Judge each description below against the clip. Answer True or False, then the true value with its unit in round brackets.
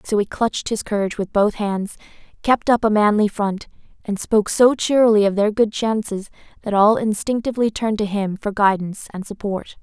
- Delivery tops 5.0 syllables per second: True (5.5 syllables/s)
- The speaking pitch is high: True (210 Hz)